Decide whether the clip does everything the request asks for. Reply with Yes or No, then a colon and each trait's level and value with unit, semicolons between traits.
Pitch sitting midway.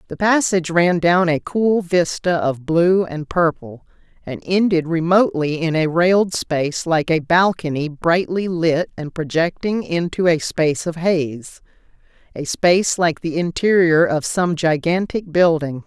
Yes: medium, 170 Hz